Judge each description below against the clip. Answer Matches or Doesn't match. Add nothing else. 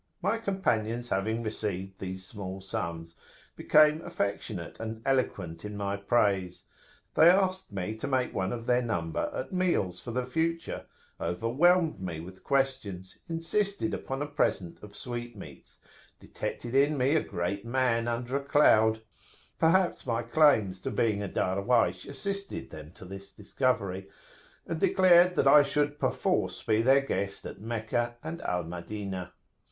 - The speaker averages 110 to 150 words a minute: Matches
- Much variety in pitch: Matches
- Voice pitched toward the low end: Matches